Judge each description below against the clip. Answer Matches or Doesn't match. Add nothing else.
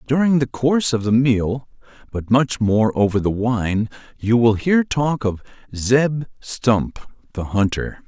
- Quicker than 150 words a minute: Doesn't match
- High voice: Doesn't match